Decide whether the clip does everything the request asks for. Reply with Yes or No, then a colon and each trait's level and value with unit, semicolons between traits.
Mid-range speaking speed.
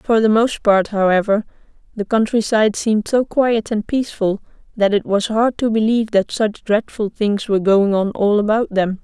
Yes: average, 185 wpm